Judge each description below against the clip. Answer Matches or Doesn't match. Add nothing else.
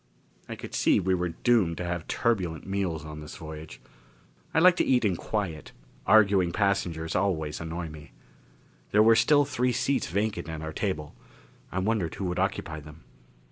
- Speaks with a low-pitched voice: Matches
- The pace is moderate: Matches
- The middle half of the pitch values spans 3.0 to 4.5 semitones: Doesn't match